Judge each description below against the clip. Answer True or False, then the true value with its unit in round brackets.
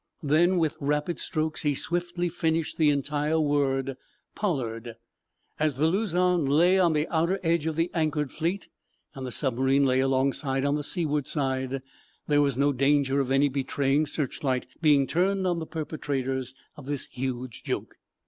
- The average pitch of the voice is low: False (145 Hz)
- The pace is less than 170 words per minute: True (160 wpm)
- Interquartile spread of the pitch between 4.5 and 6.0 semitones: False (3.3 semitones)